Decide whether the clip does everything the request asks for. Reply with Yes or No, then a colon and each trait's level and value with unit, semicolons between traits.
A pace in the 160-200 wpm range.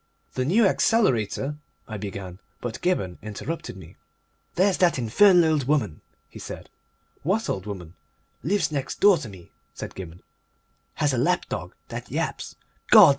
No: average, 150 wpm